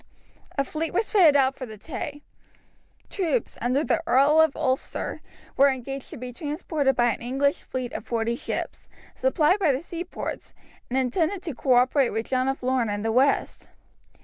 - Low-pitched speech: No, very high, 270 Hz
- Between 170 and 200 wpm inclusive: Yes, average, 175 wpm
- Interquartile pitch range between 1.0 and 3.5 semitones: No, average, 4.0 semitones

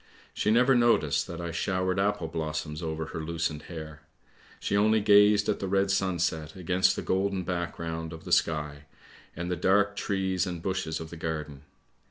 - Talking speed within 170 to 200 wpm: Yes, average, 175 wpm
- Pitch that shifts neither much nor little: Yes, average, 3.5 semitones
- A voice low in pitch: Yes, very low, 85 Hz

